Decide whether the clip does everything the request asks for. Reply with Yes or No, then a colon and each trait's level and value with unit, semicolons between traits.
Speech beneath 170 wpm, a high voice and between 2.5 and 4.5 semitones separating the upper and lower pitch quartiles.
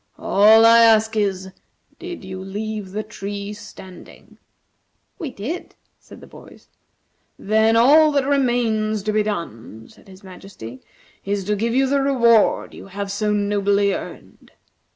Yes: average, 145 wpm; high, 210 Hz; average, 2.8 semitones